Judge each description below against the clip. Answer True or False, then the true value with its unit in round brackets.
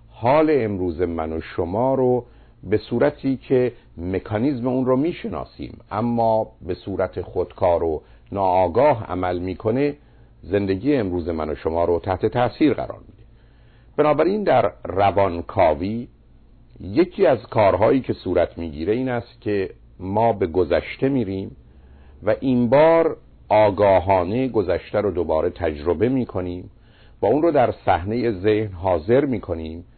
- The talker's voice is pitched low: True (105 Hz)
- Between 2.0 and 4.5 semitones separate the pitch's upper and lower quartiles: False (5.1 semitones)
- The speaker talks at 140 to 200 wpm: False (130 wpm)